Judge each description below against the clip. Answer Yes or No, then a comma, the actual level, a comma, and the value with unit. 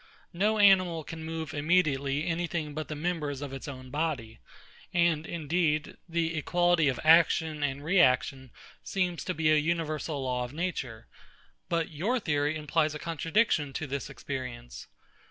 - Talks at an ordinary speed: Yes, average, 155 wpm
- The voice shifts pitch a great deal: No, average, 3.0 semitones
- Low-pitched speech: No, medium, 155 Hz